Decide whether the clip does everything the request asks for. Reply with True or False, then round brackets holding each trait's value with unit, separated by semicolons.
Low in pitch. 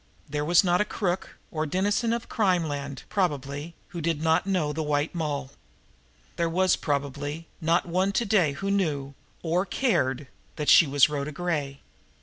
False (160 Hz)